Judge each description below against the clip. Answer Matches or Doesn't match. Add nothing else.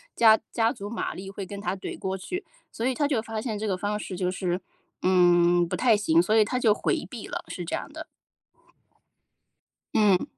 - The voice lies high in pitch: Matches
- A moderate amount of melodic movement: Matches